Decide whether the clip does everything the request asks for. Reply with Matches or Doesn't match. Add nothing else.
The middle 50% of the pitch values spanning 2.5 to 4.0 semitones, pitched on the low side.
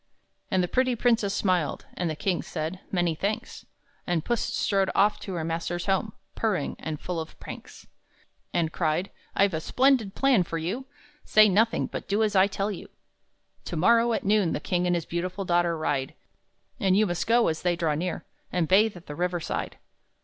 Doesn't match